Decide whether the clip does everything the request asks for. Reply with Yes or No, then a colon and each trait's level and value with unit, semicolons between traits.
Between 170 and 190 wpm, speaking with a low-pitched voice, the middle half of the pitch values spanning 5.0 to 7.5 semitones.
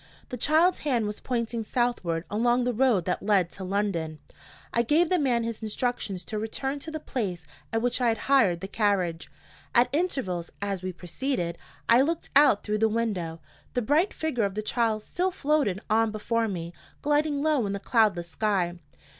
No: average, 185 wpm; high, 225 Hz; average, 5.3 semitones